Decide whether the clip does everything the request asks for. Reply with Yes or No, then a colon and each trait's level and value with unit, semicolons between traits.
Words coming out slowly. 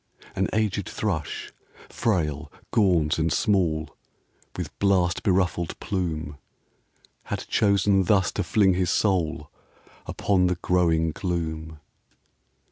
Yes: slow, 105 wpm